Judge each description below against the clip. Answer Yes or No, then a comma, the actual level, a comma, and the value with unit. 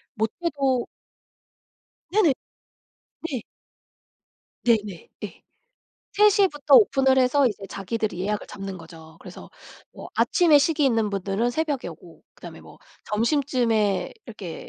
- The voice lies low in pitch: No, high, 235 Hz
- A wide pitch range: Yes, wide, 5.8 semitones